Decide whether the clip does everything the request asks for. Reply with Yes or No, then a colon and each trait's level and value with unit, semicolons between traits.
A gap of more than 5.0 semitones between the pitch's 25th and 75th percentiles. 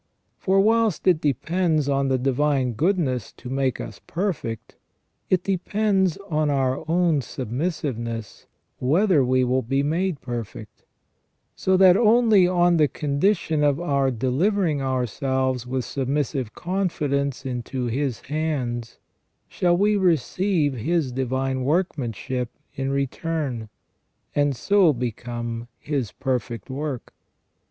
Yes: wide, 5.4 semitones